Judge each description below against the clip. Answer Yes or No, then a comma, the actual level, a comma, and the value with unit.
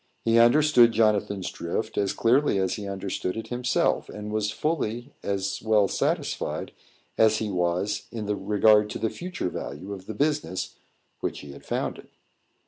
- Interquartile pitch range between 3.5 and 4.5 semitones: No, average, 2.8 semitones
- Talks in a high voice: No, low, 105 Hz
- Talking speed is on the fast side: No, average, 155 wpm